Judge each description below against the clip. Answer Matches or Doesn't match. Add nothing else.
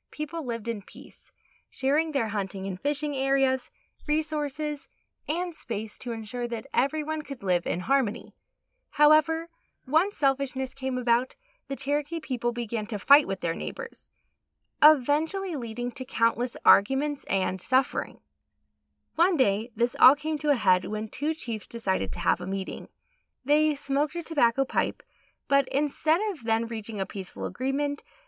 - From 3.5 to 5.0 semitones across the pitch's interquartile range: Matches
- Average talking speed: Matches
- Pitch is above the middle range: Matches